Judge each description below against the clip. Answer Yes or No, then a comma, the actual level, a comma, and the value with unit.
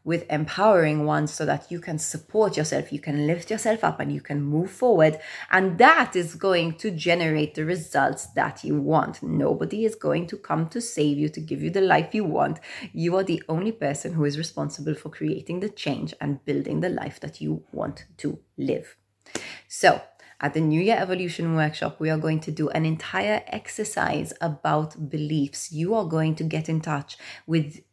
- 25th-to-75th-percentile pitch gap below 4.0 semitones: Yes, average, 3.2 semitones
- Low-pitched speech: No, medium, 160 Hz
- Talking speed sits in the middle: Yes, average, 195 wpm